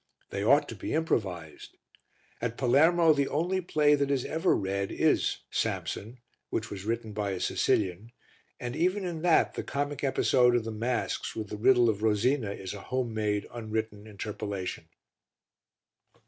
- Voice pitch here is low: Yes, low, 115 Hz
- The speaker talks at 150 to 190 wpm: Yes, average, 160 wpm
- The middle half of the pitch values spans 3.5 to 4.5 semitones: No, wide, 5.4 semitones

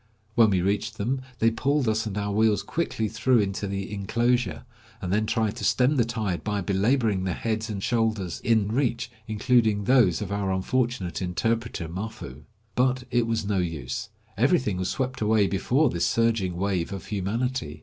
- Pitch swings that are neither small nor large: Yes, average, 3.3 semitones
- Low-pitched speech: Yes, low, 110 Hz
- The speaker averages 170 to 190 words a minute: Yes, average, 175 wpm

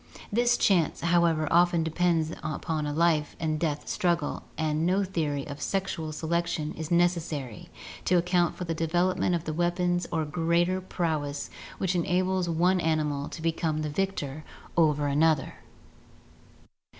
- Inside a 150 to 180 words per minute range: No, average, 140 wpm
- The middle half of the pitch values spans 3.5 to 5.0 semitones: No, narrow, 2.4 semitones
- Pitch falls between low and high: Yes, medium, 165 Hz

